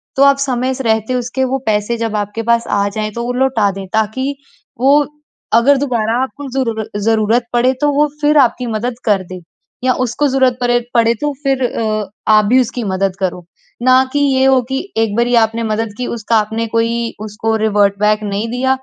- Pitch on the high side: Yes, high, 235 Hz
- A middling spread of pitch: Yes, average, 3.4 semitones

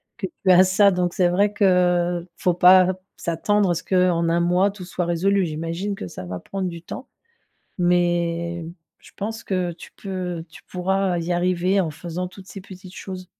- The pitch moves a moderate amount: No, narrow, 1.8 semitones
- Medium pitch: Yes, medium, 180 Hz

